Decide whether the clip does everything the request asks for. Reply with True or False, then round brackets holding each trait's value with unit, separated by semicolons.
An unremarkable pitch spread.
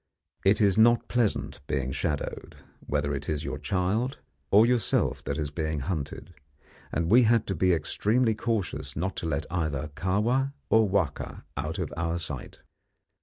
False (6.3 semitones)